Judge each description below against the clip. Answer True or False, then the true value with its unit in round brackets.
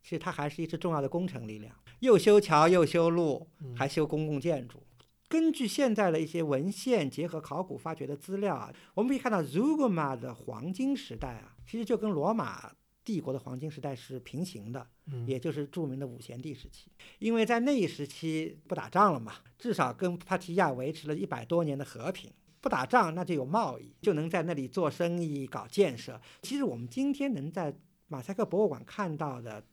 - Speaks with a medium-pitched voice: True (165 Hz)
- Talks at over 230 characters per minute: True (305 characters per minute)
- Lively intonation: True (6.1 semitones)